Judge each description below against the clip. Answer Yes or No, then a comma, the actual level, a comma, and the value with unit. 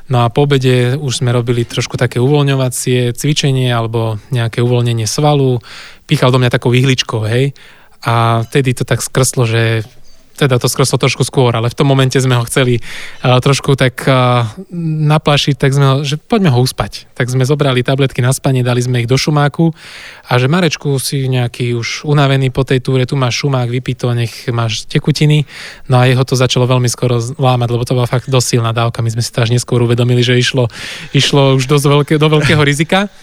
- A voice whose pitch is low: Yes, low, 130 Hz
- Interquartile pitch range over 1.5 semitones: Yes, narrow, 2.5 semitones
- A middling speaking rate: No, fast, 200 wpm